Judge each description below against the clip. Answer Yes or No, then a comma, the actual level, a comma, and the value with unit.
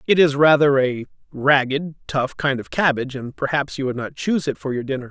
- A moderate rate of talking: No, fast, 235 wpm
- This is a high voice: No, medium, 140 Hz